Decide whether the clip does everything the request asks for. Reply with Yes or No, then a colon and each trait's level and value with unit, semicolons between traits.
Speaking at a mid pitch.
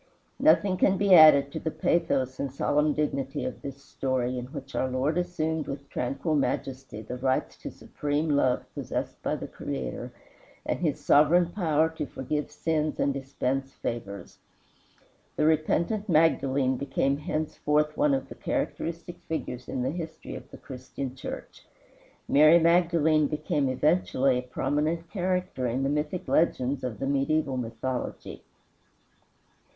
Yes: medium, 145 Hz